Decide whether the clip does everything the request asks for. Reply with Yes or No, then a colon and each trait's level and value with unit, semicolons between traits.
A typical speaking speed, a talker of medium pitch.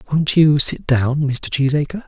Yes: average, 175 wpm; medium, 145 Hz